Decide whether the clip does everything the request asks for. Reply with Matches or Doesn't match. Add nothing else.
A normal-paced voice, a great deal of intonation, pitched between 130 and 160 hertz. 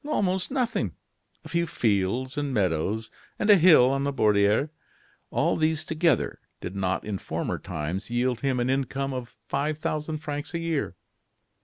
Matches